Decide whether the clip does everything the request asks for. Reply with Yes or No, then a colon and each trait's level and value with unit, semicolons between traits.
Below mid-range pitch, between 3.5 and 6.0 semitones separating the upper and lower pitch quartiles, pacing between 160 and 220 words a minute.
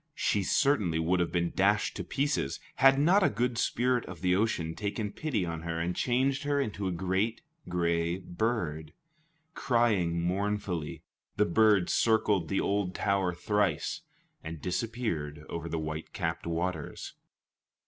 No: very low, 95 Hz; average, 4.9 semitones; average, 150 wpm